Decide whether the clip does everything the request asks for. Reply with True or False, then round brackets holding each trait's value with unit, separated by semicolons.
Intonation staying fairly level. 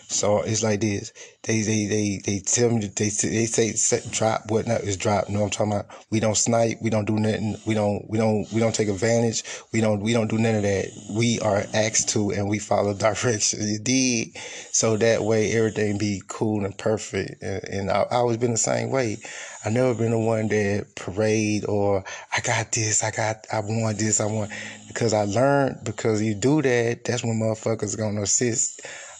True (1.4 semitones)